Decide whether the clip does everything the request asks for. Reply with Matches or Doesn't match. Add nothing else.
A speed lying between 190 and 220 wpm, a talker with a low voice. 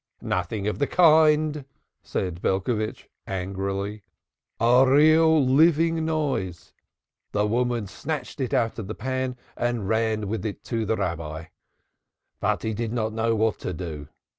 Doesn't match